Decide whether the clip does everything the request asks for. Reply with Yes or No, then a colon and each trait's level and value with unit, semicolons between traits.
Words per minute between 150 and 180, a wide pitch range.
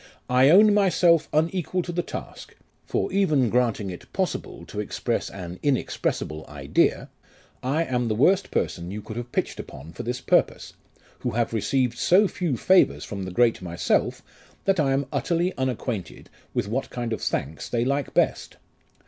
Yes: average, 165 wpm; wide, 8.0 semitones